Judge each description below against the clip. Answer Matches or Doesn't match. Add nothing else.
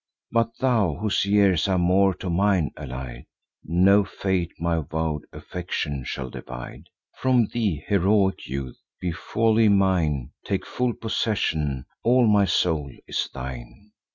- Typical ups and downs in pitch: Doesn't match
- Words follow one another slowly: Matches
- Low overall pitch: Matches